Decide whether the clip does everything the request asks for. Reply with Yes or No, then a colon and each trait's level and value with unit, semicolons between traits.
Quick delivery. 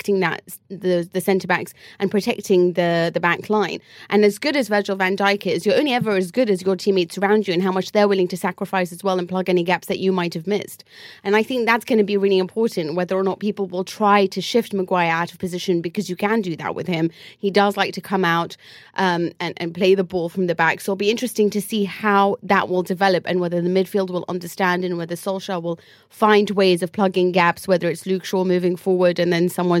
Yes: fast, 250 wpm